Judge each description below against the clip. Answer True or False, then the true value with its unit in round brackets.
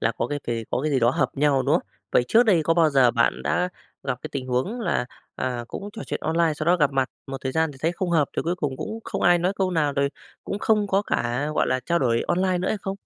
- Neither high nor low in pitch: True (150 Hz)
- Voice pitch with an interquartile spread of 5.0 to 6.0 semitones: True (5.4 semitones)